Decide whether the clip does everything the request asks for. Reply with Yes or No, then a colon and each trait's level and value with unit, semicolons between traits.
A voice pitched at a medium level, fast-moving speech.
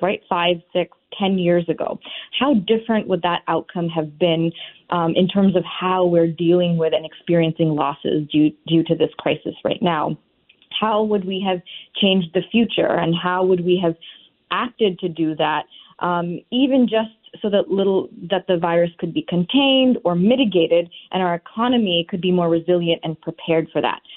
No: medium, 175 Hz; average, 180 wpm